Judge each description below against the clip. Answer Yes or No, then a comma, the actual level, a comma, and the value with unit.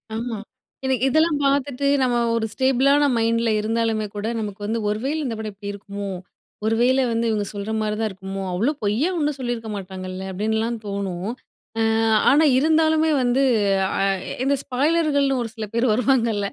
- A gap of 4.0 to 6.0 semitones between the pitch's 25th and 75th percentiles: Yes, average, 4.5 semitones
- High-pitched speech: Yes, high, 230 Hz